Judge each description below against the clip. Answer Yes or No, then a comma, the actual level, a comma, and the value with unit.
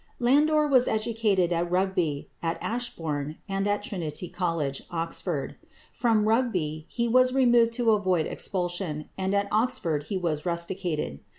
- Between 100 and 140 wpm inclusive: Yes, slow, 135 wpm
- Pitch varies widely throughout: Yes, wide, 5.7 semitones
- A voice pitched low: No, high, 190 Hz